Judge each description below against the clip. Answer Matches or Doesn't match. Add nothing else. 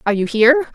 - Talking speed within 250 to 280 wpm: Doesn't match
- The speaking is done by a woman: Matches